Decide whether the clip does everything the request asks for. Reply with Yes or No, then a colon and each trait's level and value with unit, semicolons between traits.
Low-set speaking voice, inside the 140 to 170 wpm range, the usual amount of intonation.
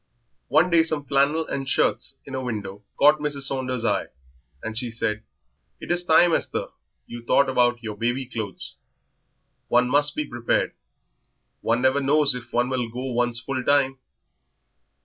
Yes: low, 130 Hz; average, 160 wpm; average, 3.2 semitones